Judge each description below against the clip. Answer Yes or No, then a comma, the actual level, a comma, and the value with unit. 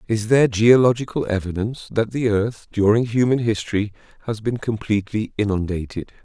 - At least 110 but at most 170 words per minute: Yes, slow, 135 wpm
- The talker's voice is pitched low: Yes, low, 110 Hz